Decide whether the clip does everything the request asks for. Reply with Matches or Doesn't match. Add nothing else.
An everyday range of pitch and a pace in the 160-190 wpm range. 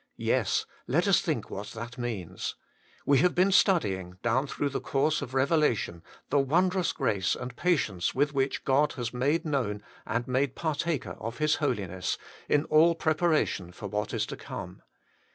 Doesn't match